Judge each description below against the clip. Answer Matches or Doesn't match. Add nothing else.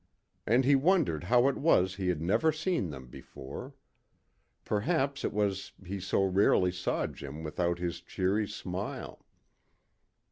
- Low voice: Matches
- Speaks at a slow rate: Doesn't match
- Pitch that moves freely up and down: Matches